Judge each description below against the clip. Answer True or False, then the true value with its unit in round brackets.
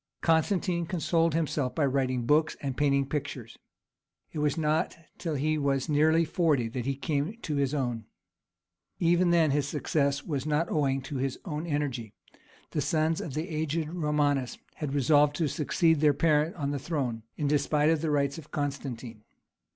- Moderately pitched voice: True (150 Hz)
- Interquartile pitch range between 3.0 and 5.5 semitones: False (2.5 semitones)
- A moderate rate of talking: True (170 wpm)